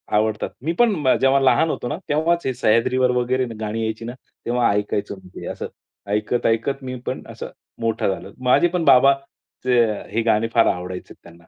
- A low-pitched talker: Yes, low, 120 Hz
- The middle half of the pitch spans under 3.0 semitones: No, average, 3.7 semitones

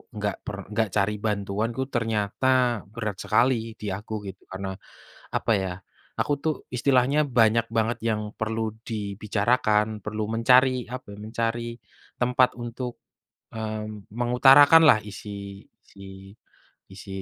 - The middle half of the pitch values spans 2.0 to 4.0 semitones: Yes, average, 2.8 semitones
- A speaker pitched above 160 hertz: No, low, 110 Hz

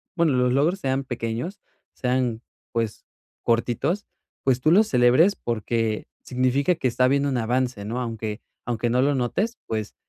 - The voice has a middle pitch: No, low, 125 Hz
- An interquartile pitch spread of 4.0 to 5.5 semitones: No, average, 3.2 semitones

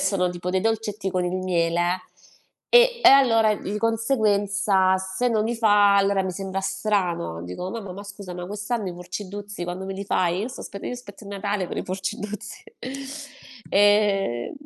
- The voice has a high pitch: Yes, high, 200 Hz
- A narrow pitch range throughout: Yes, narrow, 2.3 semitones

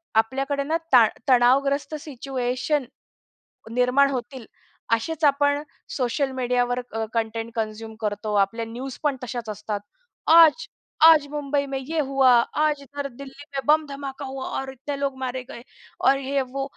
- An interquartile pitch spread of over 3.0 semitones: No, average, 2.7 semitones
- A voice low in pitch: No, very high, 270 Hz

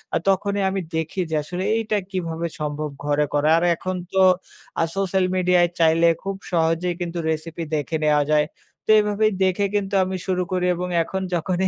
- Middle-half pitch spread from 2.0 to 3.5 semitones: Yes, average, 2.9 semitones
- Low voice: No, medium, 180 Hz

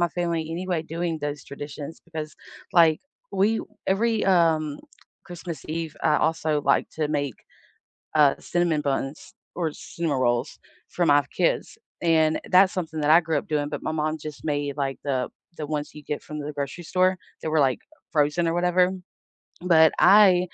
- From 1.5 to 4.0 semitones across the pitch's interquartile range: Yes, average, 2.9 semitones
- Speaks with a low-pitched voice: No, medium, 155 Hz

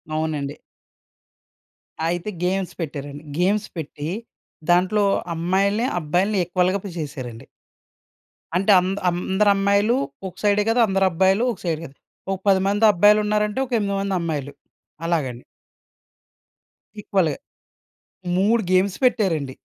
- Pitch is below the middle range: No, high, 190 Hz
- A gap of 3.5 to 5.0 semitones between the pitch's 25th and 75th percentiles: Yes, average, 4.1 semitones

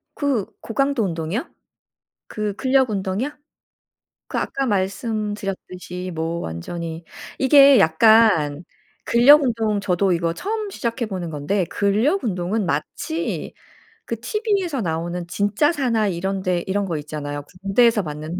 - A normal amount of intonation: No, wide, 5.8 semitones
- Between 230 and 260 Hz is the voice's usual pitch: No, high, 200 Hz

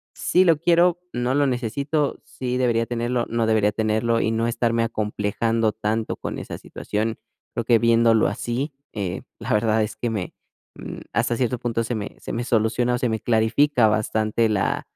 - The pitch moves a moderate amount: No, narrow, 1.9 semitones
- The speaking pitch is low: Yes, low, 115 Hz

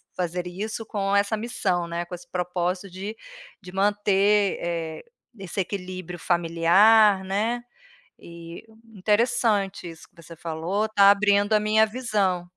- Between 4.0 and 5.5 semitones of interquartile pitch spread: No, average, 3.0 semitones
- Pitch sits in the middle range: No, high, 195 Hz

